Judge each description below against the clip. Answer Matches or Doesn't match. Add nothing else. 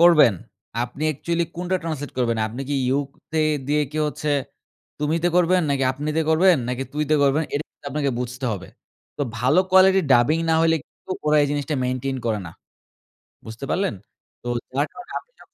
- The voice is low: Doesn't match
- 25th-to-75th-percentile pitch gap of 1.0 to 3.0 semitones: Doesn't match